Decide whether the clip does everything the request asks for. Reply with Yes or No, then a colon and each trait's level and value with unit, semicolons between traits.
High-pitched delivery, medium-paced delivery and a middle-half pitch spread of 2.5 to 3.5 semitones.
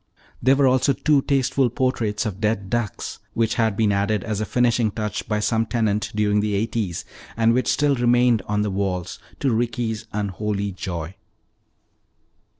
No: low, 110 Hz; average, 160 wpm; average, 2.8 semitones